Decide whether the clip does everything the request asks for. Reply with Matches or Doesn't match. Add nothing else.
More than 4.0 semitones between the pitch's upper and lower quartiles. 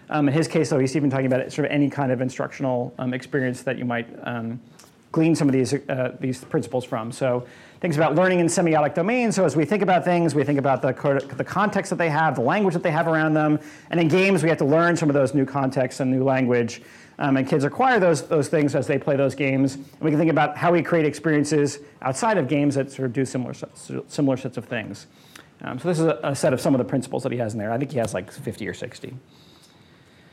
Doesn't match